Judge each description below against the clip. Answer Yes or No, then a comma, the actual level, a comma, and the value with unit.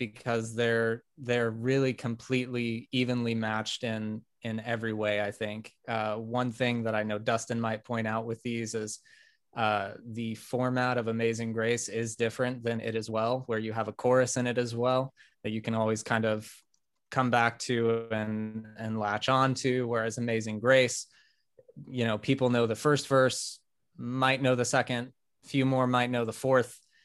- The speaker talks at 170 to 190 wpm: Yes, average, 180 wpm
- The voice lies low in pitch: Yes, low, 115 Hz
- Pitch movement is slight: Yes, narrow, 2.2 semitones